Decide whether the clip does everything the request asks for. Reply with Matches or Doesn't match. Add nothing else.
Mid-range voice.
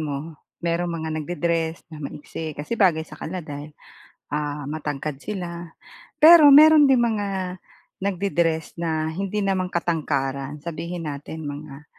Matches